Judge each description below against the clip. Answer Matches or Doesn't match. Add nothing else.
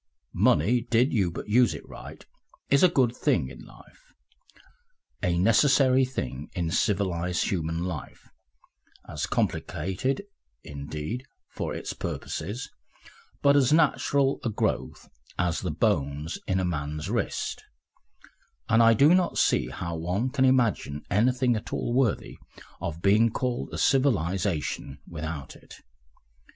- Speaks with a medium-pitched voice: Doesn't match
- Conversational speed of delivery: Doesn't match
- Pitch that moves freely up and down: Matches